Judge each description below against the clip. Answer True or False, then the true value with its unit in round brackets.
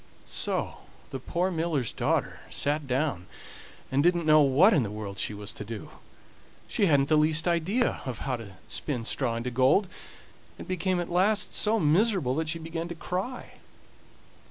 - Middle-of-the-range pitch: True (155 Hz)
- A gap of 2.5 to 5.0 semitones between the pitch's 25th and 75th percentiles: False (5.5 semitones)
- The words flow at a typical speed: True (170 wpm)